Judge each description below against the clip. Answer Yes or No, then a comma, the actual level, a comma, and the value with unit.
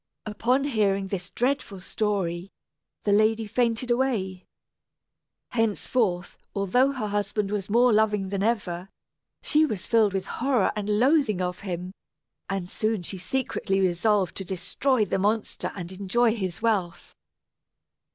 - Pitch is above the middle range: Yes, high, 205 Hz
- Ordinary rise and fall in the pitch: Yes, average, 3.4 semitones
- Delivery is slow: Yes, slow, 130 wpm